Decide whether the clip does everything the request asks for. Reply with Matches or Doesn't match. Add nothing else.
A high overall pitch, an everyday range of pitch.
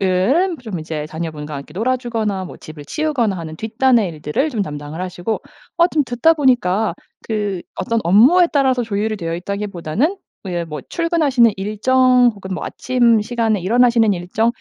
Doesn't match